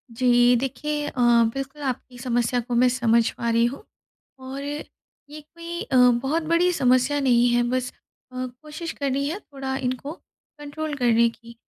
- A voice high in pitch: Yes, very high, 260 Hz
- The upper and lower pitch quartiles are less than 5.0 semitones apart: Yes, average, 3.3 semitones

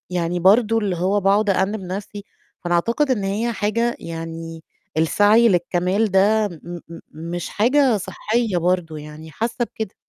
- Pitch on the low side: No, high, 195 Hz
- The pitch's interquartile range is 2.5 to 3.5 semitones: No, average, 4.0 semitones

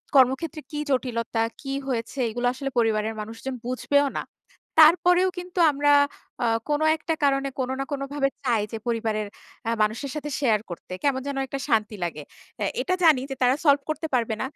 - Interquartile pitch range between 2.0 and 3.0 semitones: No, average, 4.2 semitones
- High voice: Yes, very high, 265 Hz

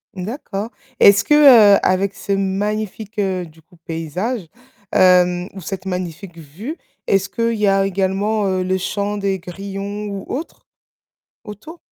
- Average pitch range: No, narrow, 2.3 semitones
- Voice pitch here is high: Yes, high, 195 Hz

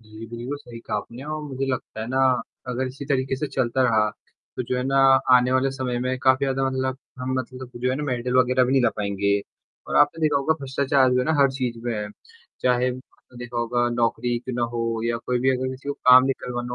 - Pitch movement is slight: Yes, narrow, 1.7 semitones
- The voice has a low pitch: Yes, low, 125 Hz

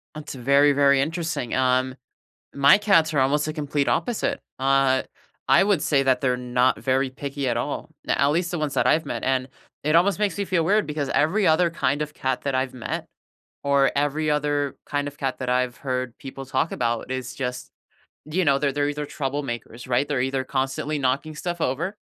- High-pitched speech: No, medium, 140 Hz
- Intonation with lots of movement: No, average, 2.7 semitones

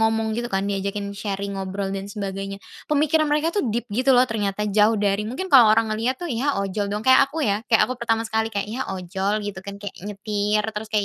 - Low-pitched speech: No, high, 210 Hz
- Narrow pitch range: No, average, 3.0 semitones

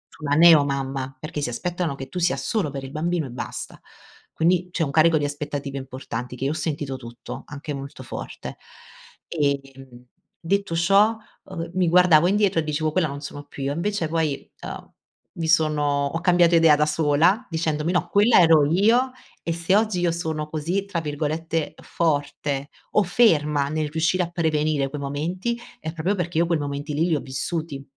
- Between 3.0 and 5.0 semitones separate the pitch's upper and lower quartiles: Yes, average, 3.3 semitones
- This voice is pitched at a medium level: Yes, medium, 155 Hz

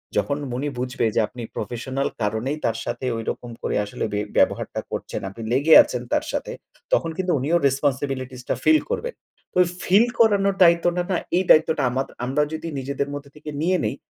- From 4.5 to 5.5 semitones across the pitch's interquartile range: Yes, average, 5.2 semitones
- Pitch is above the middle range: No, medium, 140 Hz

